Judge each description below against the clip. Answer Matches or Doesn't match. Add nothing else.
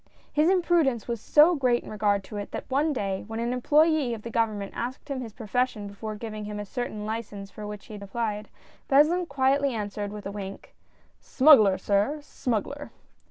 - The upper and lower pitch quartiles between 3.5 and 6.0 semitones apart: Matches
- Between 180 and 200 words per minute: Matches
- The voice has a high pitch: Matches